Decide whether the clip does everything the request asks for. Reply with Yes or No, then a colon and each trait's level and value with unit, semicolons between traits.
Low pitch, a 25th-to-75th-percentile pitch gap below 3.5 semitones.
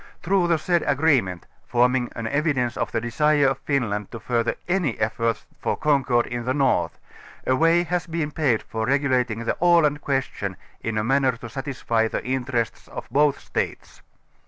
No: low, 130 Hz; average, 4.2 semitones